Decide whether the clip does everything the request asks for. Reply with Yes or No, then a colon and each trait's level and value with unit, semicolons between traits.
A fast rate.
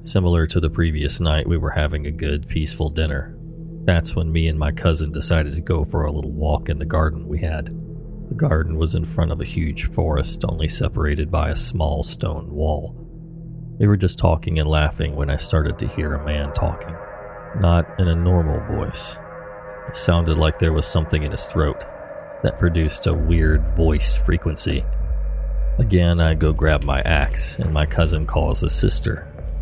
No: average, 185 wpm